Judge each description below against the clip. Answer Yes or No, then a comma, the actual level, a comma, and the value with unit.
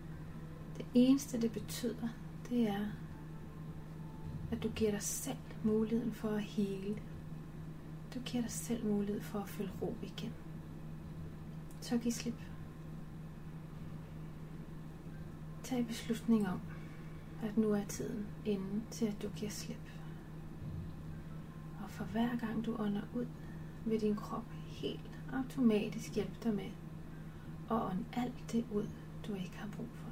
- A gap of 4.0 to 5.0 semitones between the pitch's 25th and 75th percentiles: Yes, average, 4.3 semitones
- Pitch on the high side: Yes, high, 210 Hz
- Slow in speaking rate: Yes, slow, 130 wpm